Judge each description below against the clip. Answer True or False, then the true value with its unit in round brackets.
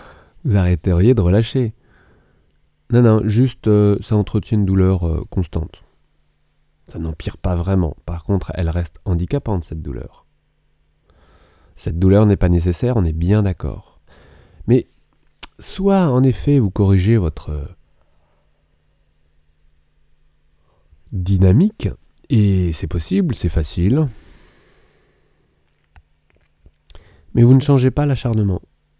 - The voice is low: True (90 Hz)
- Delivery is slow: True (110 wpm)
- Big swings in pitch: True (5.7 semitones)